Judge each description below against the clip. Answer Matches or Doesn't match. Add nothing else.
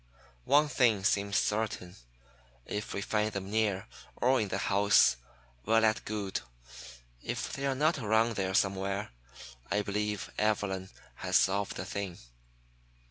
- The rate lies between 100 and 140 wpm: Matches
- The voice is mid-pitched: Doesn't match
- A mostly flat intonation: Matches